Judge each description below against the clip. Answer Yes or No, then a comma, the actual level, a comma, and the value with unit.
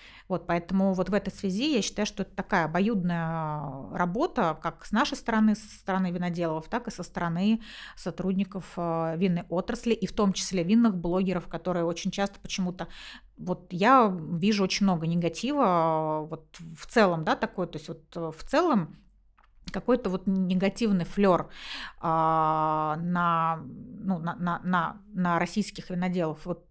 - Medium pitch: Yes, medium, 180 Hz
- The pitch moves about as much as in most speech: Yes, average, 3.2 semitones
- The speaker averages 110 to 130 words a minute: No, average, 150 wpm